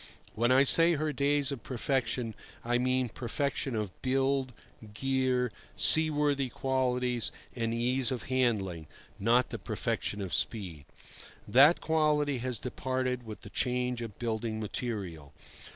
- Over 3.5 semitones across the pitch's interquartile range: No, average, 2.7 semitones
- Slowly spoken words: Yes, slow, 130 wpm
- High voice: No, low, 125 Hz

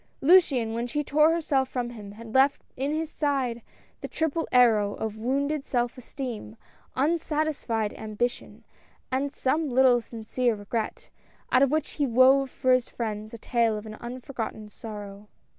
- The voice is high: Yes, very high, 250 Hz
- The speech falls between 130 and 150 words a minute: No, average, 160 wpm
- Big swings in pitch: No, average, 3.9 semitones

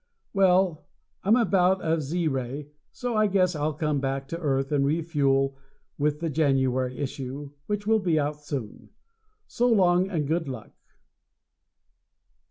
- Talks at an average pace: Yes, average, 150 wpm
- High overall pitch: No, medium, 155 Hz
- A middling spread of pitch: Yes, average, 4.8 semitones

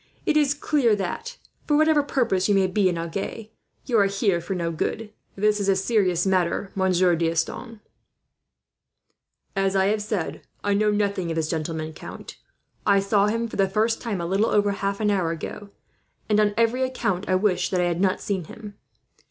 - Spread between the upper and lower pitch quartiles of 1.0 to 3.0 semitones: Yes, average, 2.7 semitones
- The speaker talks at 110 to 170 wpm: No, average, 195 wpm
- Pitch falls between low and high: No, high, 200 Hz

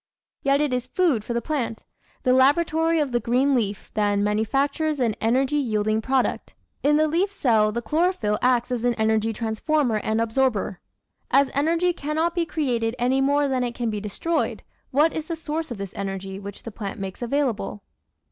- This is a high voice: Yes, very high, 250 Hz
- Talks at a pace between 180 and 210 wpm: Yes, average, 185 wpm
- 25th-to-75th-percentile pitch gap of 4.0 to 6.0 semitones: Yes, average, 5.2 semitones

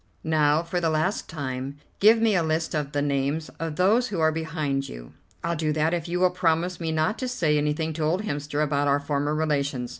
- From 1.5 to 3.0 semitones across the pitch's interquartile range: Yes, average, 2.7 semitones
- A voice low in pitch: No, medium, 155 Hz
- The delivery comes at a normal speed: No, fast, 220 wpm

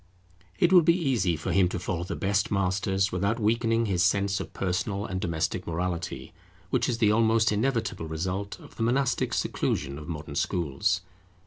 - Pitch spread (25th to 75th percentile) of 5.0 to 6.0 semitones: No, average, 4.1 semitones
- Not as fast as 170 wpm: No, average, 175 wpm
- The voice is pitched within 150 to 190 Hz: No, very low, 95 Hz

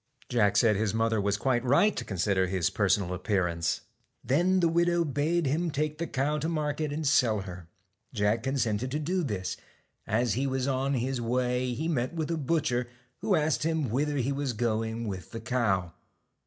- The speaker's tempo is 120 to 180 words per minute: No, average, 190 wpm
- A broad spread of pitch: Yes, wide, 5.8 semitones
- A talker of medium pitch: No, low, 125 Hz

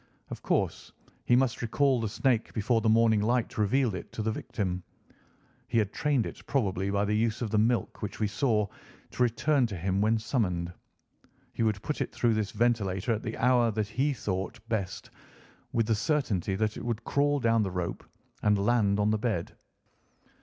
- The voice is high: No, low, 110 Hz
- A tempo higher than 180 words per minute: Yes, average, 190 wpm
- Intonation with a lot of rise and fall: No, average, 2.9 semitones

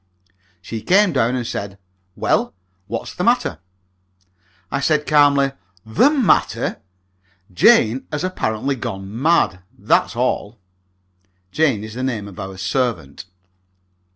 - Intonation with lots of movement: Yes, wide, 6.1 semitones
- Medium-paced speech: No, slow, 120 wpm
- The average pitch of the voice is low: Yes, low, 120 Hz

